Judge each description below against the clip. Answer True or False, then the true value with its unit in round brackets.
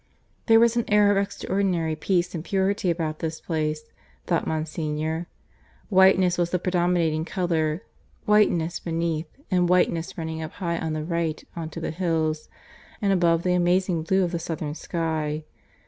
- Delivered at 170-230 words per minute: False (160 wpm)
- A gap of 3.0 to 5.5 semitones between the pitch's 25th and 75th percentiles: False (2.5 semitones)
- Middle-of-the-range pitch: True (170 Hz)